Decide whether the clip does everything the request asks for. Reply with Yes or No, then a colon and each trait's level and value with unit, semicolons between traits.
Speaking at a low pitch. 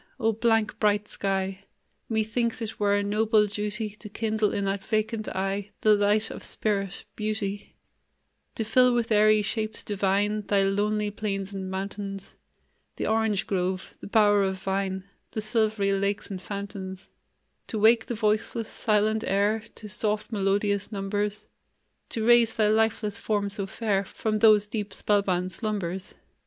No: high, 210 Hz